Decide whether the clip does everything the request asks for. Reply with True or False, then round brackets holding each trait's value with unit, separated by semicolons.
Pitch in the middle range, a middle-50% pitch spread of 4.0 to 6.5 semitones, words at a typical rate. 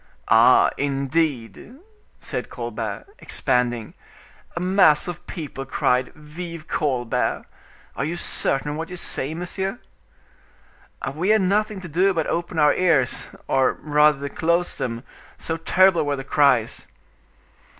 False (155 Hz; 4.5 semitones; 130 wpm)